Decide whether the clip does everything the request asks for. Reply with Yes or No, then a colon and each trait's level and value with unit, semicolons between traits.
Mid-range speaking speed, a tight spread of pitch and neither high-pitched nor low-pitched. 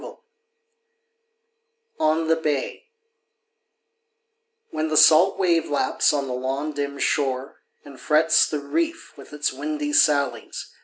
No: slow, 125 wpm; narrow, 2.1 semitones; medium, 150 Hz